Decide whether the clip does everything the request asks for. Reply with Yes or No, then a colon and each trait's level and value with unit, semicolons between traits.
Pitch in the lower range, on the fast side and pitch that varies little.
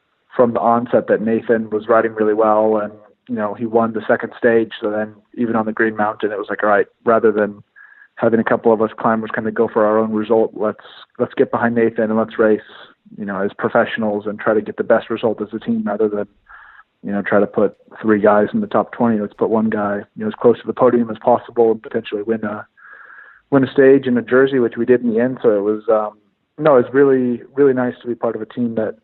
Yes: low, 115 Hz; fast, 260 wpm; narrow, 1.7 semitones